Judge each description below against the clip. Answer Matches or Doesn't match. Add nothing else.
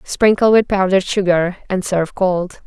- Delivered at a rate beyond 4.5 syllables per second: Matches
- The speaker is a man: Doesn't match